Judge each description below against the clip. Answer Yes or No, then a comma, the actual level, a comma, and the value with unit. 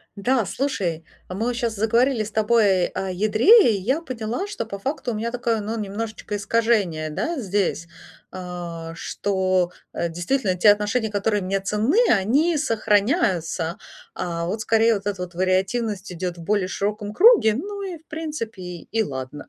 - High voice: Yes, high, 210 Hz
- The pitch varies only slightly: No, average, 4.2 semitones